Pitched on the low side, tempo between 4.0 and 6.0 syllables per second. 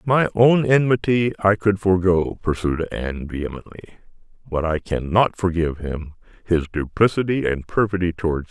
Yes: very low, 95 Hz; 5.3 syllables/s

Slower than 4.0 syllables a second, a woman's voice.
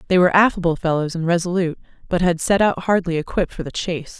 No: 7.1 syllables/s; female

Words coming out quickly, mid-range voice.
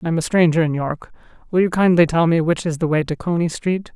Yes: fast, 275 wpm; medium, 165 Hz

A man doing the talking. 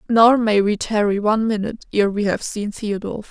No: female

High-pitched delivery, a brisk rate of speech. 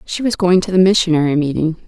No: medium, 170 Hz; fast, 225 wpm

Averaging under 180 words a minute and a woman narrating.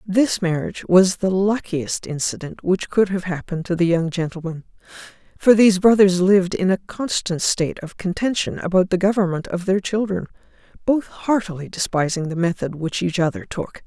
Yes: average, 170 wpm; female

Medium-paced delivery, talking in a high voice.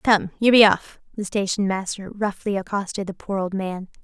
Yes: average, 195 wpm; high, 195 Hz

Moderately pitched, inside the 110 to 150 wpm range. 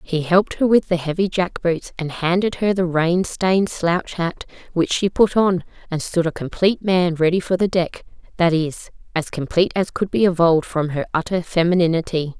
No: medium, 175 Hz; average, 195 wpm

